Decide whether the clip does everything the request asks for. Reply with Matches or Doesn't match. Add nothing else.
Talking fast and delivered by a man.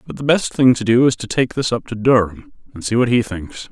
Matches